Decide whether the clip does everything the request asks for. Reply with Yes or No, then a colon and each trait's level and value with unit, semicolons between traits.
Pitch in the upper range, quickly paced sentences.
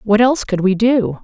Yes: high, 220 Hz; fast, 240 wpm